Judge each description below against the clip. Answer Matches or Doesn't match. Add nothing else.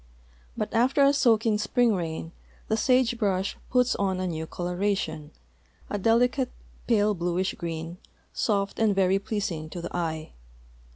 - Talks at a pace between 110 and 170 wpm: Matches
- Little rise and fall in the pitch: Doesn't match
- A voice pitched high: Matches